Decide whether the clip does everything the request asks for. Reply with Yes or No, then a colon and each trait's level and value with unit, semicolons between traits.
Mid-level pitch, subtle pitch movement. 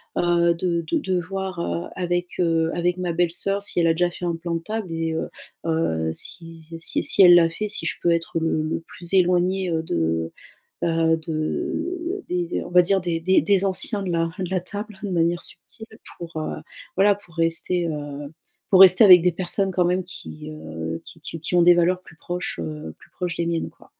Yes: medium, 175 Hz; narrow, 2.0 semitones